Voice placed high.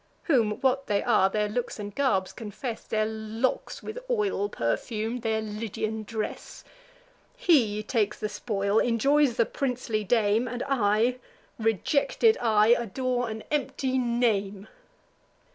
Yes: high, 225 Hz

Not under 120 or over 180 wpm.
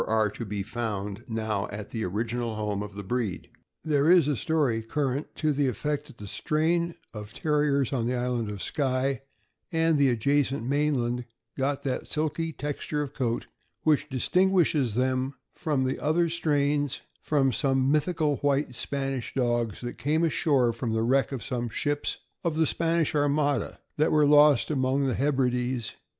Yes: average, 165 wpm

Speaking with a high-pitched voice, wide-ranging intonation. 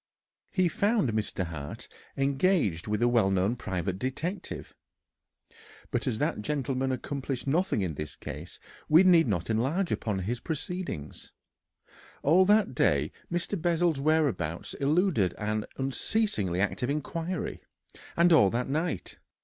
No: low, 135 Hz; wide, 8.5 semitones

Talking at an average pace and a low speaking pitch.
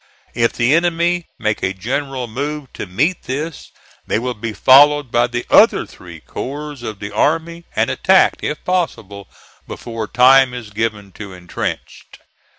Yes: average, 155 wpm; low, 125 Hz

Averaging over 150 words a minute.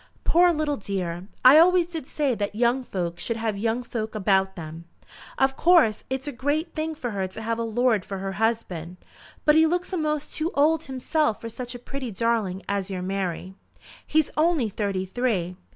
Yes: average, 190 wpm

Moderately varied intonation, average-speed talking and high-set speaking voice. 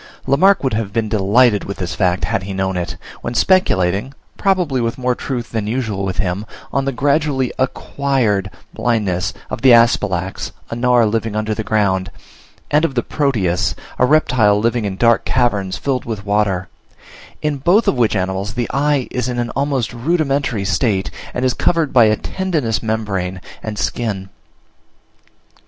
No: average, 4.8 semitones; average, 165 wpm; low, 115 Hz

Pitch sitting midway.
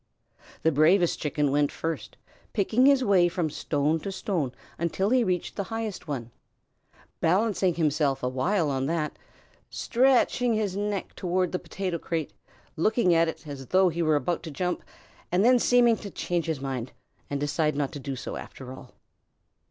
Yes: medium, 170 Hz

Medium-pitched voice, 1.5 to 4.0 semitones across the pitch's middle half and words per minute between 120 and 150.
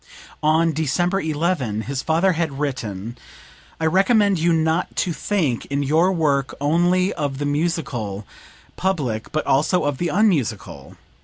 No: medium, 155 Hz; average, 4.5 semitones; average, 140 wpm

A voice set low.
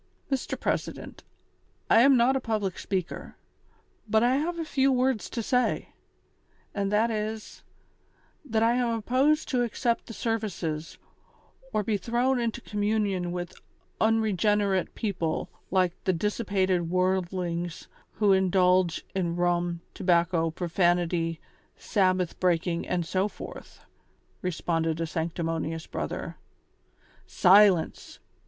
No: high, 190 Hz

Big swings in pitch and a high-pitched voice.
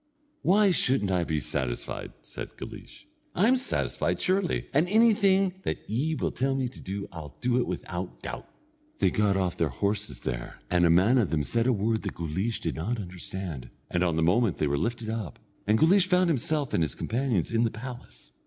No: wide, 7.9 semitones; low, 110 Hz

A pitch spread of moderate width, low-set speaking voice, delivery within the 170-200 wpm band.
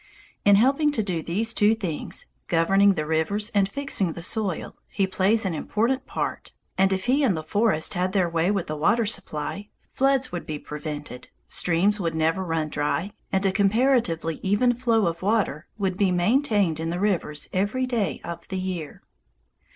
No: average, 4.7 semitones; high, 190 Hz; average, 180 wpm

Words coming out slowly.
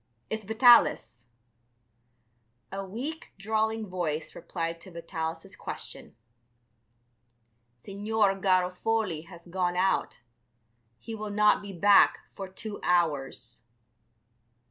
Yes: slow, 95 wpm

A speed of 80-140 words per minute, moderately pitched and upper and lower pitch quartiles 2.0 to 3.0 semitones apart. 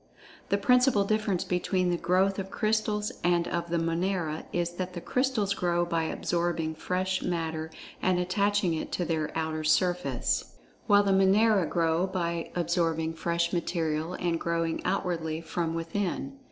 No: average, 155 wpm; medium, 175 Hz; narrow, 2.6 semitones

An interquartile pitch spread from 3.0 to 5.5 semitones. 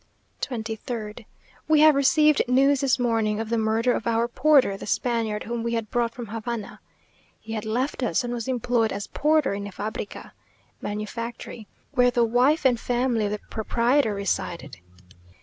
No: narrow, 2.5 semitones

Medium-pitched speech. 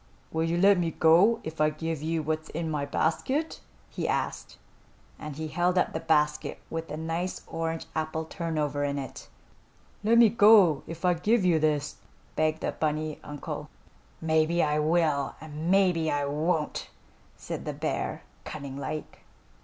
Yes: medium, 160 Hz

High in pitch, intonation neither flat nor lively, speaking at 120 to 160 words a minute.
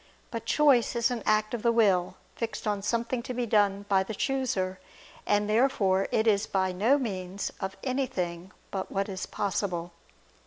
No: high, 210 Hz; average, 3.6 semitones; average, 170 wpm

